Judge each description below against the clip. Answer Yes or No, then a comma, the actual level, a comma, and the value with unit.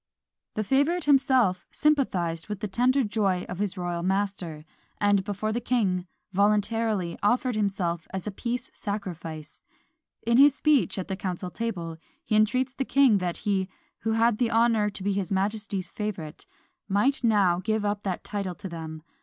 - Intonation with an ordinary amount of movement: Yes, average, 3.9 semitones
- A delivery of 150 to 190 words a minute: Yes, average, 165 wpm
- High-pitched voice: Yes, high, 205 Hz